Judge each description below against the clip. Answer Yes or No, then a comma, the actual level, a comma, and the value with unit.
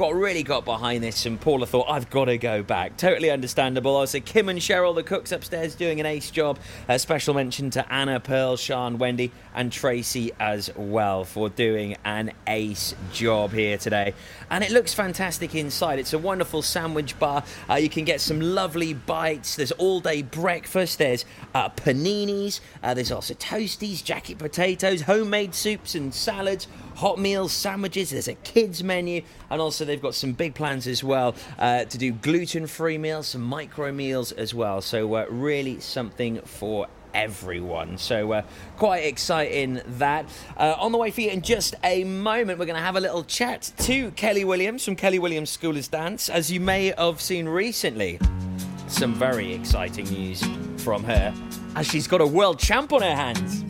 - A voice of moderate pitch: Yes, medium, 150 Hz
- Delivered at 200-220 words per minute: No, average, 185 wpm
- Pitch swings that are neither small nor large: No, wide, 6.9 semitones